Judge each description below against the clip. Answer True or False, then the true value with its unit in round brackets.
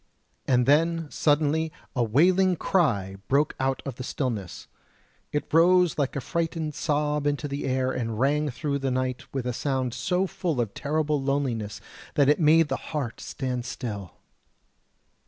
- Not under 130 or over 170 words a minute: True (155 wpm)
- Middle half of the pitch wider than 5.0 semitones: False (3.4 semitones)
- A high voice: False (140 Hz)